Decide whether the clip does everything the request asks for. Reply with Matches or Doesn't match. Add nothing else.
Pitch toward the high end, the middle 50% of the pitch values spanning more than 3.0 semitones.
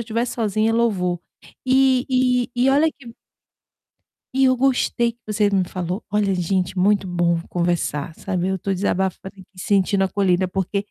Matches